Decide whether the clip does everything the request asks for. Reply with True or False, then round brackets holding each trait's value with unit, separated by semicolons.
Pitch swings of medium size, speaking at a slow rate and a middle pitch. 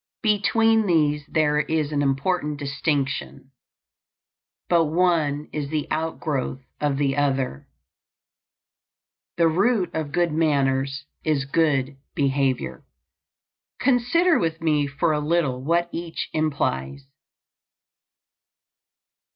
True (3.2 semitones; 100 wpm; 150 Hz)